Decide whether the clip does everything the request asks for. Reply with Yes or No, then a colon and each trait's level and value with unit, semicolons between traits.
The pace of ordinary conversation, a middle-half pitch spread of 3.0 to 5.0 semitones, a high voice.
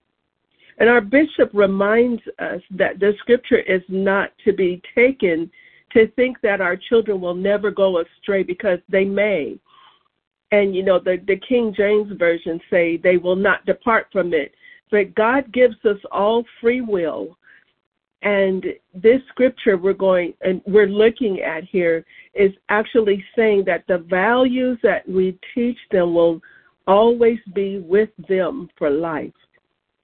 Yes: average, 150 wpm; average, 3.5 semitones; high, 200 Hz